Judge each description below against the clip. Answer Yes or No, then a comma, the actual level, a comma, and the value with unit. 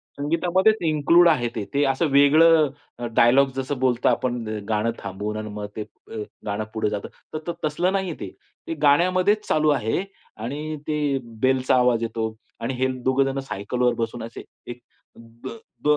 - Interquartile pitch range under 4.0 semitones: No, average, 4.9 semitones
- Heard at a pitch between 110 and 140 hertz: Yes, low, 135 Hz